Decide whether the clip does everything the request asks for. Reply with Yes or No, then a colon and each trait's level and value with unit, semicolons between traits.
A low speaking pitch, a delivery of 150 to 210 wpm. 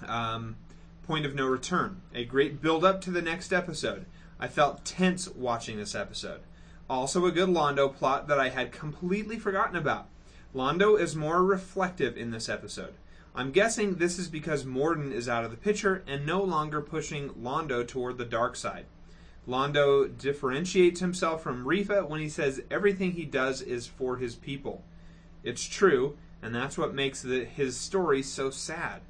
No: medium, 145 Hz; average, 170 wpm